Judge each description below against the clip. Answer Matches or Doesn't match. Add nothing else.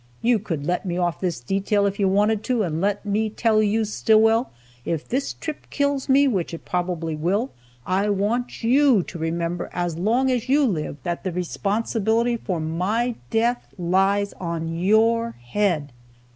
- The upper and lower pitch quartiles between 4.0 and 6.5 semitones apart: Matches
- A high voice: Matches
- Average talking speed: Matches